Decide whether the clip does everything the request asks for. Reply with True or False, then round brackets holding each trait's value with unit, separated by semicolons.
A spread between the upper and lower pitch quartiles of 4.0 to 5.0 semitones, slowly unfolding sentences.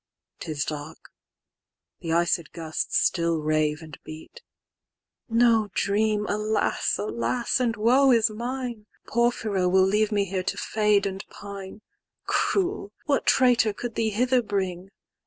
True (4.5 semitones; 120 wpm)